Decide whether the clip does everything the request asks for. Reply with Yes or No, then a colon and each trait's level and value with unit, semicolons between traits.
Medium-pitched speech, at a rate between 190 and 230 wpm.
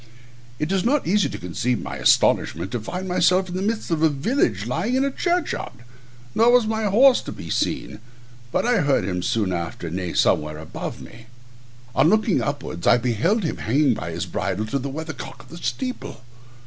Yes: medium, 150 Hz; average, 200 wpm